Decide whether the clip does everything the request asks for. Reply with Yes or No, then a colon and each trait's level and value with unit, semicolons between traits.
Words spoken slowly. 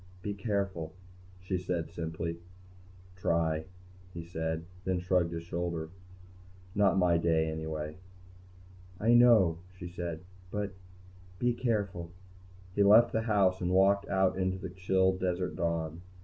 Yes: slow, 125 wpm